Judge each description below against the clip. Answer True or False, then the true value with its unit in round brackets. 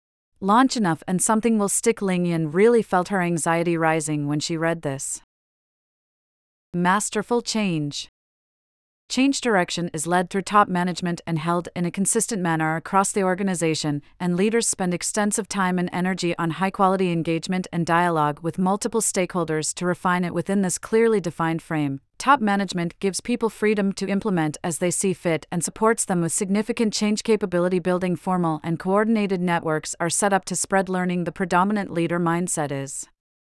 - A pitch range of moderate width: True (3.3 semitones)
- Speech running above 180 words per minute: False (165 wpm)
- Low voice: False (180 Hz)